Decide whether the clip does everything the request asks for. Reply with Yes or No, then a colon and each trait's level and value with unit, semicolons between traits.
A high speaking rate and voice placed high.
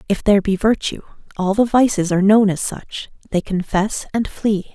No: average, 190 wpm; high, 200 Hz